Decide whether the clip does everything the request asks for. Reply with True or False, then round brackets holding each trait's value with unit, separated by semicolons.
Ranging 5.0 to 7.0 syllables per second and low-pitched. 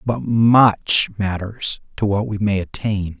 False (3.5 syllables/s; 105 Hz)